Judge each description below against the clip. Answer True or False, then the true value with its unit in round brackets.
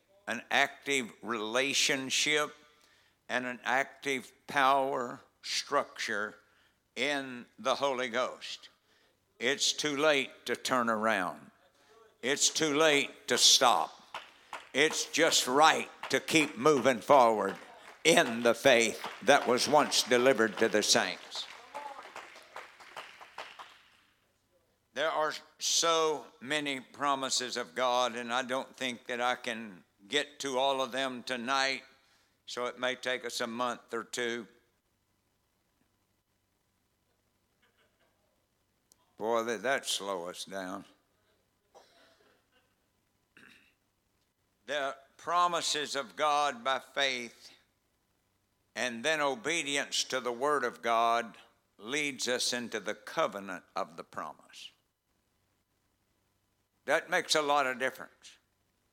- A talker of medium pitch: False (125 Hz)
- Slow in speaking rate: True (105 wpm)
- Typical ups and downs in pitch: True (3.8 semitones)